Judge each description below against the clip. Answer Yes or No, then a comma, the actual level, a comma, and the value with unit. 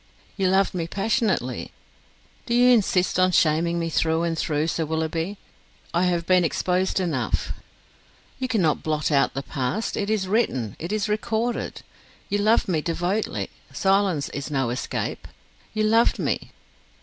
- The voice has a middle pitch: Yes, medium, 180 Hz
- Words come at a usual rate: Yes, average, 150 wpm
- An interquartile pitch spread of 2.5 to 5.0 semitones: Yes, average, 4.6 semitones